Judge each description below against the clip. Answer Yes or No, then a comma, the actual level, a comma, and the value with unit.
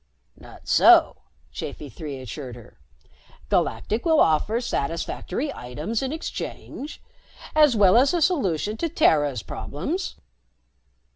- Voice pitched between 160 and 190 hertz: No, high, 205 Hz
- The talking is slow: Yes, slow, 115 wpm